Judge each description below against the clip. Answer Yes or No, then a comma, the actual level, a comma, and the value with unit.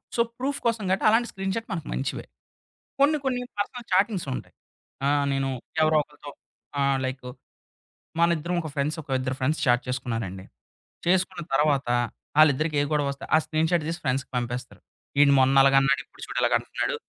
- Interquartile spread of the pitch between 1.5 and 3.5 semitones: No, average, 5.3 semitones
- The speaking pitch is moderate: Yes, medium, 150 Hz